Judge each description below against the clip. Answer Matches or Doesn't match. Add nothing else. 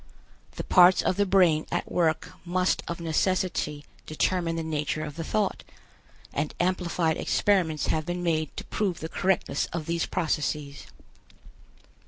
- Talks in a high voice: Doesn't match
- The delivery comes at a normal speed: Matches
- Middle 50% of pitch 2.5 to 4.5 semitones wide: Matches